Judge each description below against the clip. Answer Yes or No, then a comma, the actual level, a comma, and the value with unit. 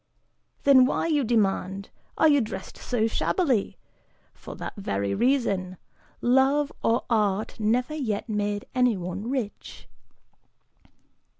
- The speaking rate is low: Yes, slow, 110 wpm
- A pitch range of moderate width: Yes, average, 4.8 semitones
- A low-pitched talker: No, high, 225 Hz